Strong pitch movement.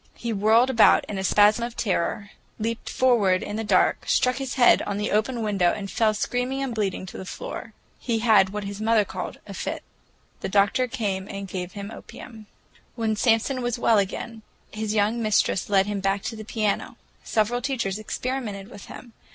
No: average, 2.9 semitones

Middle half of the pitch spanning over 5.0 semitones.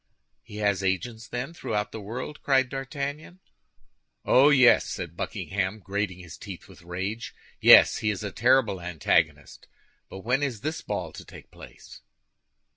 Yes: wide, 5.4 semitones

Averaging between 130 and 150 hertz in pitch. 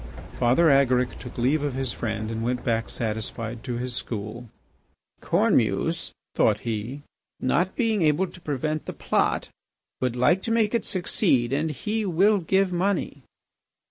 Yes: low, 135 Hz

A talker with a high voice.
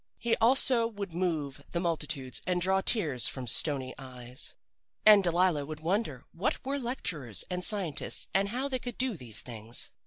No: medium, 175 Hz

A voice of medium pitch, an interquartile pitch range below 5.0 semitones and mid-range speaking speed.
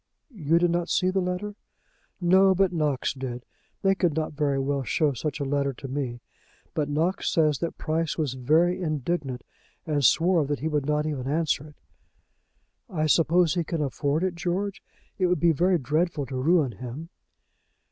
Yes: medium, 155 Hz; average, 3.7 semitones; average, 180 wpm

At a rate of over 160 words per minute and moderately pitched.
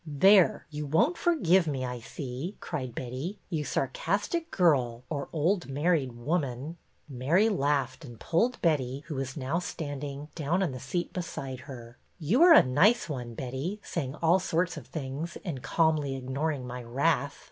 Yes: average, 175 wpm; medium, 145 Hz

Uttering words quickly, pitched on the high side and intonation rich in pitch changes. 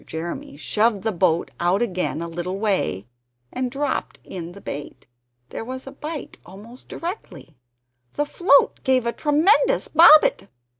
No: average, 145 wpm; high, 225 Hz; wide, 8.6 semitones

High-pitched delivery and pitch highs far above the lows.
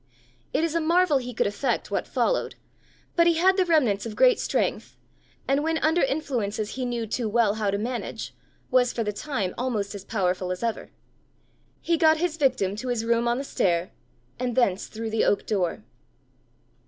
Yes: high, 240 Hz; wide, 6.8 semitones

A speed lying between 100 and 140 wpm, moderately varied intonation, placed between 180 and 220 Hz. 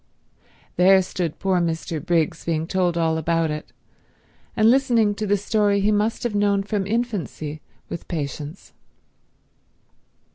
Yes: slow, 135 wpm; average, 4.1 semitones; high, 190 Hz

